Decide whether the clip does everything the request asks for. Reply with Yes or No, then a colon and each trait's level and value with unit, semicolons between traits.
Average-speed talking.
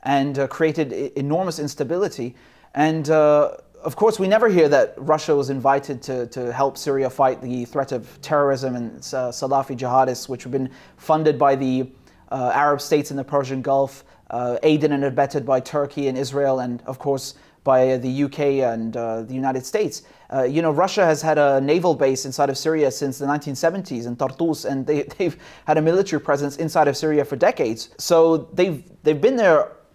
Yes: average, 190 wpm